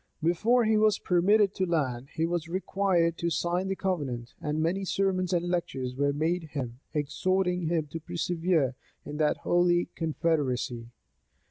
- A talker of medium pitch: Yes, medium, 170 Hz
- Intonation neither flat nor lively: Yes, average, 3.6 semitones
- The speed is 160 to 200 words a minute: No, average, 150 wpm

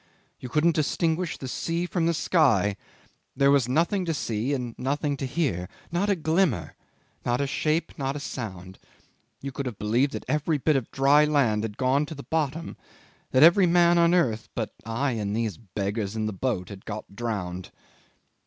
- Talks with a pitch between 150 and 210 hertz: No, low, 135 Hz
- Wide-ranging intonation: Yes, wide, 6.3 semitones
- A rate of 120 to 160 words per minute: No, average, 185 wpm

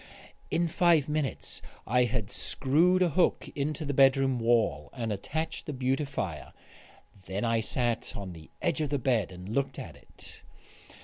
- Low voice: Yes, low, 130 Hz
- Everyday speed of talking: Yes, average, 160 wpm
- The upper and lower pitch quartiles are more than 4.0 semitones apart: Yes, average, 5.1 semitones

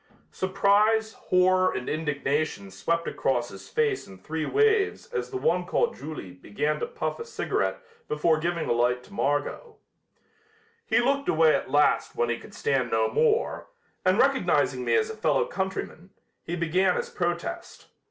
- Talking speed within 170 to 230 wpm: No, average, 160 wpm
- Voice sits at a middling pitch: Yes, medium, 170 Hz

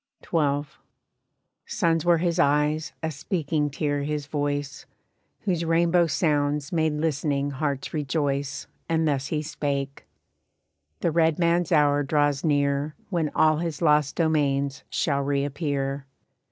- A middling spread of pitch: No, narrow, 2.2 semitones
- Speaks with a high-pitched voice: No, medium, 150 Hz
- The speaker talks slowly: Yes, slow, 125 wpm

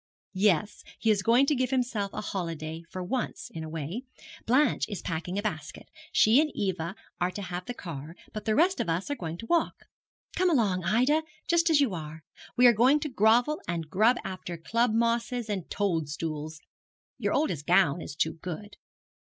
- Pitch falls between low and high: No, high, 200 Hz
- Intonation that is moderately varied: No, wide, 6.5 semitones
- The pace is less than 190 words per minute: No, average, 195 wpm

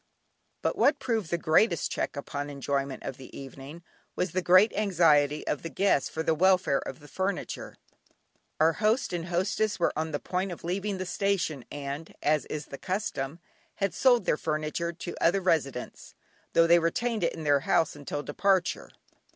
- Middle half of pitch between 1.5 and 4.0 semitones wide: No, average, 4.4 semitones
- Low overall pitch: No, medium, 165 Hz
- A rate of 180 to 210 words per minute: Yes, average, 185 wpm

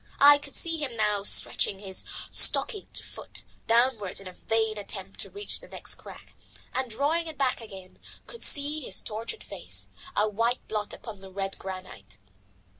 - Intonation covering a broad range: Yes, wide, 6.3 semitones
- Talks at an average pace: Yes, average, 170 wpm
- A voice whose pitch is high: Yes, high, 225 Hz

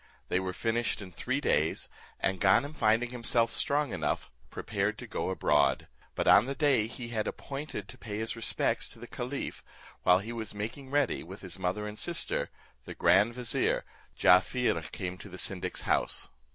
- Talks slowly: No, average, 180 wpm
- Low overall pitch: Yes, low, 110 Hz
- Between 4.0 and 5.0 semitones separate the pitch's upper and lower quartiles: Yes, average, 4.7 semitones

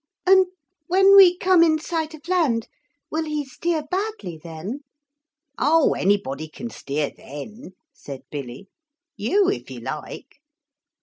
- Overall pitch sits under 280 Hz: No, very high, 300 Hz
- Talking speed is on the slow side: Yes, slow, 130 wpm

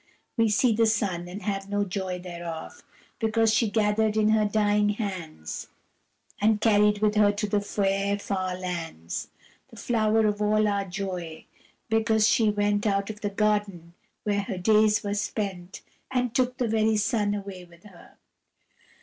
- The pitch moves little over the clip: Yes, narrow, 1.9 semitones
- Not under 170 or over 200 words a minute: No, average, 160 wpm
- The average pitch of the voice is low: No, high, 205 Hz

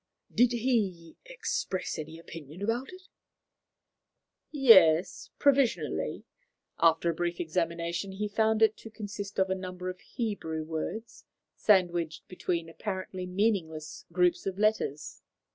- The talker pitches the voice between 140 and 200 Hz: Yes, medium, 185 Hz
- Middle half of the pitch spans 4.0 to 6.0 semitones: Yes, average, 4.5 semitones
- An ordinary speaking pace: No, slow, 120 wpm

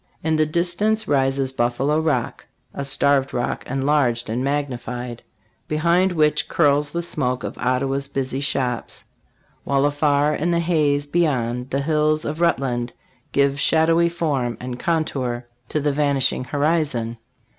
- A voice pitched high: No, medium, 140 Hz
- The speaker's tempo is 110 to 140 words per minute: Yes, slow, 135 wpm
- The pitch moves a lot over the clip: No, average, 3.3 semitones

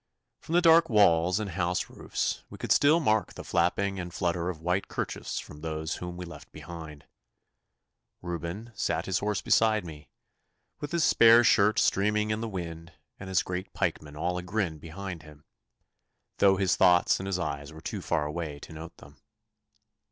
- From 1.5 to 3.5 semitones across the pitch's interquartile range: No, average, 3.9 semitones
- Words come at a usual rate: Yes, average, 175 wpm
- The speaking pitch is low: Yes, very low, 90 Hz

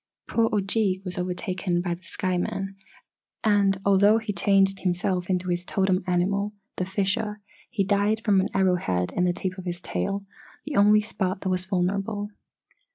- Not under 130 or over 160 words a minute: No, average, 170 wpm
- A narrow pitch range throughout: Yes, narrow, 2.0 semitones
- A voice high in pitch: Yes, high, 195 Hz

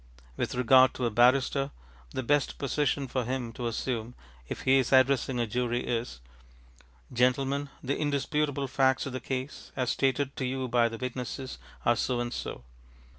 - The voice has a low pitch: Yes, low, 130 Hz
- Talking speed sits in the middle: Yes, average, 170 wpm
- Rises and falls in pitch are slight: Yes, narrow, 1.9 semitones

